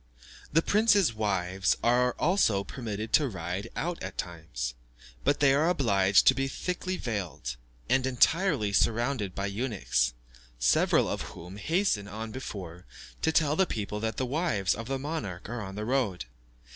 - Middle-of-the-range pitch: No, low, 110 Hz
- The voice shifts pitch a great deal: Yes, wide, 6.4 semitones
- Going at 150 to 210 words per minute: Yes, average, 160 wpm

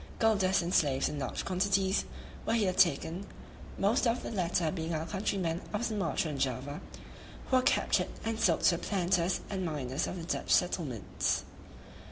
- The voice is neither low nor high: Yes, medium, 180 Hz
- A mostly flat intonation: No, average, 3.7 semitones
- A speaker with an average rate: Yes, average, 175 wpm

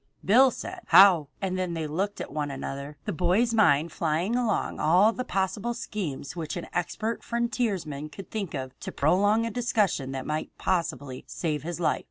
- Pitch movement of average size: No, wide, 5.8 semitones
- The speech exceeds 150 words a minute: Yes, average, 180 wpm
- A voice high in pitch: No, medium, 180 Hz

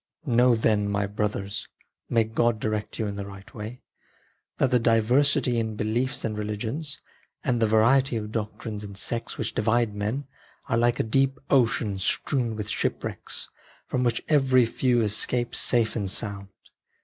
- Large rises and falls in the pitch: No, narrow, 2.6 semitones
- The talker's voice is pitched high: No, low, 115 Hz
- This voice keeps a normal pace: Yes, average, 160 wpm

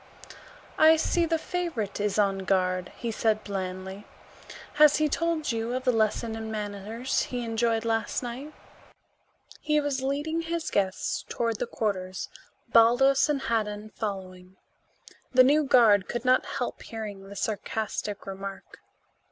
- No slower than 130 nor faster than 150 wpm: Yes, average, 140 wpm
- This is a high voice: Yes, high, 225 Hz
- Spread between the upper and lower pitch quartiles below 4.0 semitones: No, average, 5.0 semitones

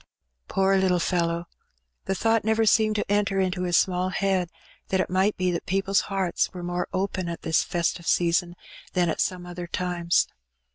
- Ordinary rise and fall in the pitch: No, narrow, 1.8 semitones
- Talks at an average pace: Yes, average, 180 wpm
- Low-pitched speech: No, medium, 185 Hz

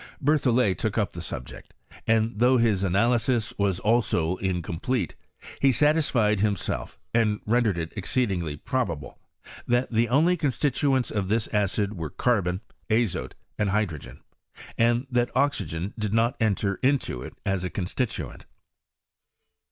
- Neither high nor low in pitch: No, low, 110 Hz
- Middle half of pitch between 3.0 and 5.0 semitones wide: Yes, average, 4.3 semitones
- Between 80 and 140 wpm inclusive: Yes, slow, 135 wpm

